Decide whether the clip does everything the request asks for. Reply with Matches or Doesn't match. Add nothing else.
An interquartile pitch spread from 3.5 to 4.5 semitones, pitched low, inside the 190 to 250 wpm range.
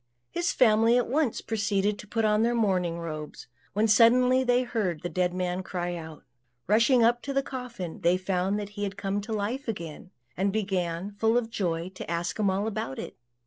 Doesn't match